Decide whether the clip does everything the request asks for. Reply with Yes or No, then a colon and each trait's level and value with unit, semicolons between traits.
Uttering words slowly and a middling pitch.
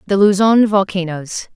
No: slow, 115 wpm; high, 195 Hz